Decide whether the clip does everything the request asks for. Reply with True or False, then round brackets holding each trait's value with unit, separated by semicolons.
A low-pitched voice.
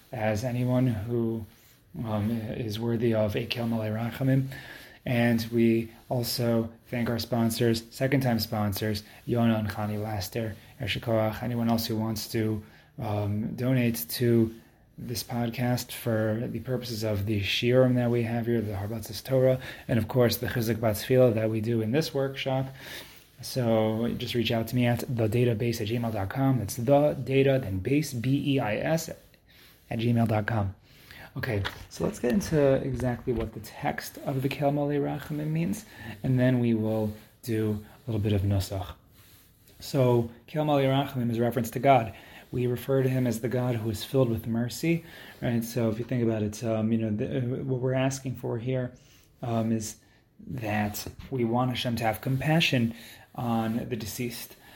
True (120 Hz)